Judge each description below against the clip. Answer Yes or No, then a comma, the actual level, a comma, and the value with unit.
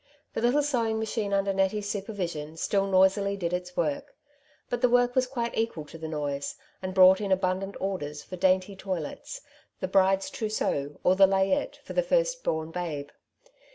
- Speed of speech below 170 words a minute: No, average, 180 wpm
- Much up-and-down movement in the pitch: No, average, 3.7 semitones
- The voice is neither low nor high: No, high, 195 Hz